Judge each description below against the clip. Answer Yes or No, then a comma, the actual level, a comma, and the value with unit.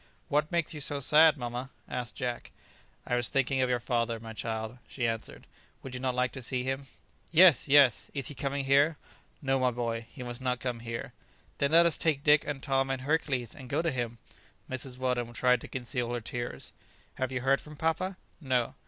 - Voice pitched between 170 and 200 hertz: No, low, 130 Hz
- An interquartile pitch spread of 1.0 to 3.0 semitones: Yes, average, 2.7 semitones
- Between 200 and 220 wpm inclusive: Yes, fast, 205 wpm